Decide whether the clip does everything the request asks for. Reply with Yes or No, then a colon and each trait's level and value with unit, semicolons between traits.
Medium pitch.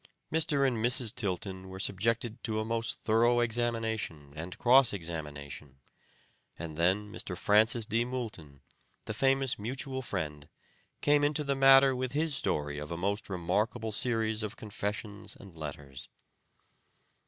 No: low, 110 Hz